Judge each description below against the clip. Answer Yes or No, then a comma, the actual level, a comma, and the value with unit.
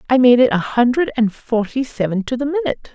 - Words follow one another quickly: Yes, fast, 225 wpm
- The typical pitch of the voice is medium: No, high, 245 Hz